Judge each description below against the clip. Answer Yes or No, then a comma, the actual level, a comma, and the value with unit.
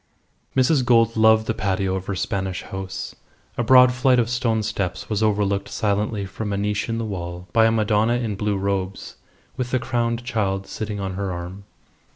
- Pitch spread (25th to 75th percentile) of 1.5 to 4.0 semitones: Yes, average, 3.0 semitones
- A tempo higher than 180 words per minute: Yes, average, 190 wpm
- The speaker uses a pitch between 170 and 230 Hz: No, low, 105 Hz